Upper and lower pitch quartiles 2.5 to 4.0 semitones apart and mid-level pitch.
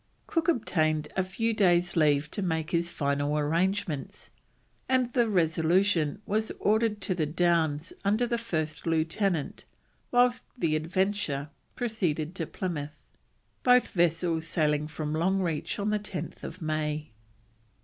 No: average, 4.8 semitones; medium, 170 Hz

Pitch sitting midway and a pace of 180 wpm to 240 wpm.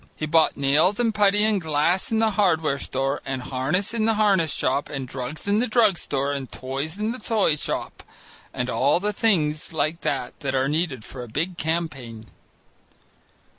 Yes: medium, 155 Hz; average, 185 wpm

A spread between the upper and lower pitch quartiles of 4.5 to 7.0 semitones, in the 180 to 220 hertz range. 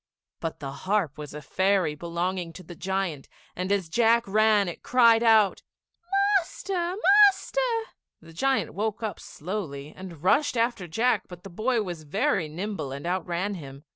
Yes: average, 5.3 semitones; high, 190 Hz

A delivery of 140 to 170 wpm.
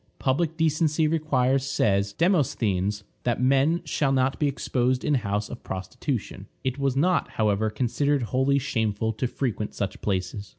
Yes: average, 145 wpm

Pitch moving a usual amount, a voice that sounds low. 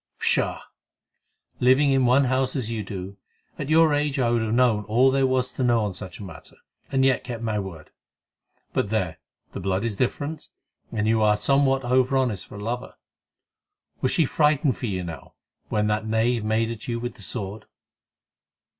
Yes: average, 3.8 semitones; low, 120 Hz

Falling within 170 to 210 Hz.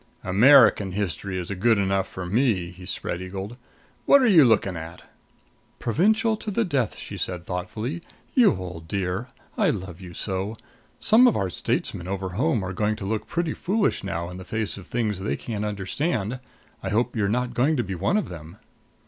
No: low, 100 Hz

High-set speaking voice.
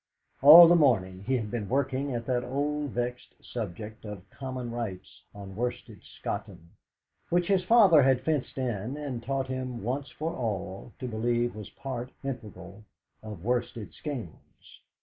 No: low, 125 Hz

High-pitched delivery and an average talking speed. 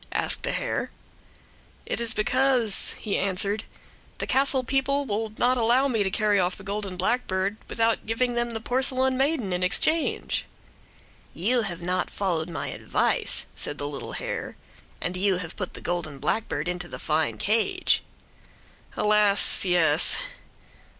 Yes: high, 205 Hz; average, 150 wpm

